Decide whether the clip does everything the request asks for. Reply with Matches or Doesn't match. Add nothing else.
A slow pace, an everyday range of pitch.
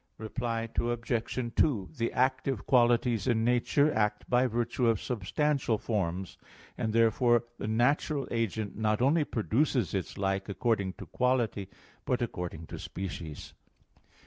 Matches